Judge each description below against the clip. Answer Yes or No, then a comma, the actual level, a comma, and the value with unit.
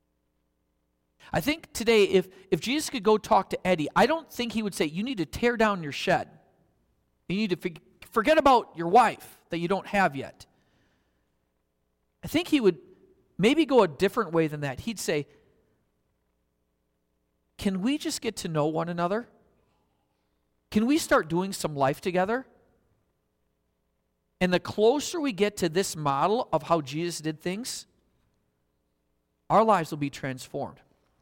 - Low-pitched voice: No, medium, 175 Hz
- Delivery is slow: No, average, 160 wpm